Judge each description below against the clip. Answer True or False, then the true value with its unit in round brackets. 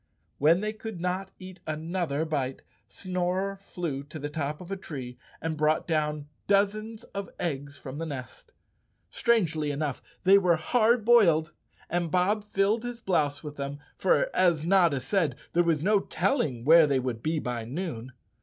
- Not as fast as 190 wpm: True (165 wpm)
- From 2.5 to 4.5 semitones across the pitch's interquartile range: False (4.9 semitones)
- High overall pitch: False (165 Hz)